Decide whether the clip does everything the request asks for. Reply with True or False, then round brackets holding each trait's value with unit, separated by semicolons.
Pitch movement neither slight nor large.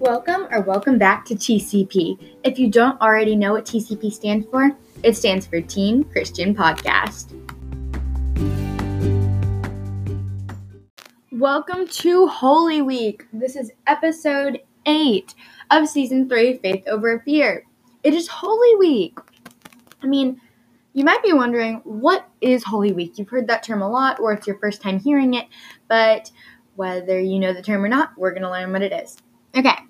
False (6.3 semitones)